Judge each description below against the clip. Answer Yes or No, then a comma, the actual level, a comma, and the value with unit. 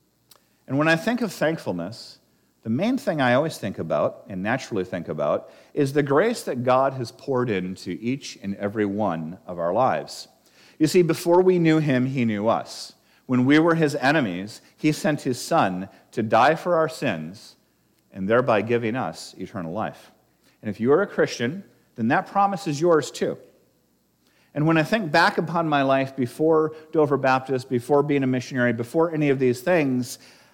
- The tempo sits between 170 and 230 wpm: Yes, average, 185 wpm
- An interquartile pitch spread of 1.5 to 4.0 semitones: No, average, 4.5 semitones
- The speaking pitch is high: No, low, 135 Hz